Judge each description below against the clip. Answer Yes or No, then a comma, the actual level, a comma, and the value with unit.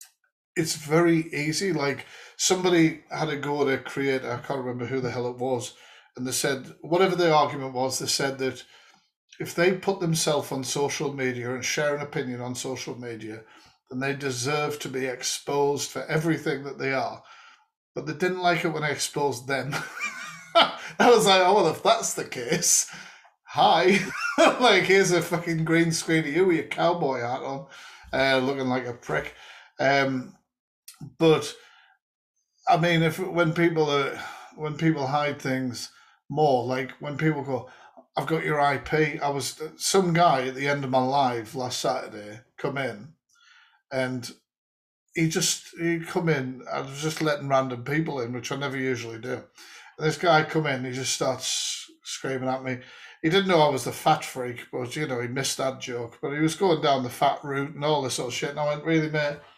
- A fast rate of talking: No, average, 190 wpm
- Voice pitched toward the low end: No, medium, 145 Hz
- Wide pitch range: No, average, 3.8 semitones